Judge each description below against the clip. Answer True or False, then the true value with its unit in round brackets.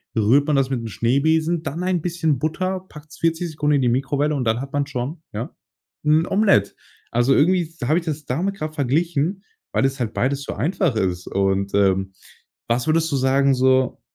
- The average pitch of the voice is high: False (140 Hz)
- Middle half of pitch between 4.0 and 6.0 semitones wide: True (4.4 semitones)